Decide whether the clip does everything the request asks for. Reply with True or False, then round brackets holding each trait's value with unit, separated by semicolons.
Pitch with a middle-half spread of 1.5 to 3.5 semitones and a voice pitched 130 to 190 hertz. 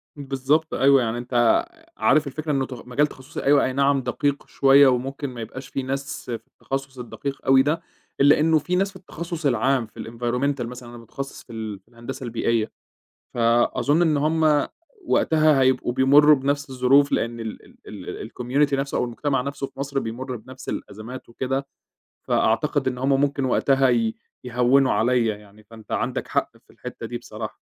True (2.7 semitones; 135 Hz)